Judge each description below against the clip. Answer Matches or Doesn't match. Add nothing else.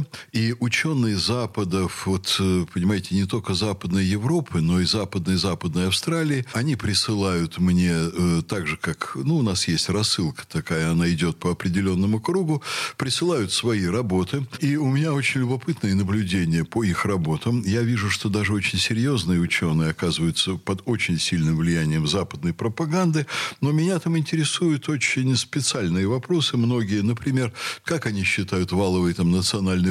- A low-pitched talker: Matches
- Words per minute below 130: Doesn't match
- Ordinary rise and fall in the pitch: Doesn't match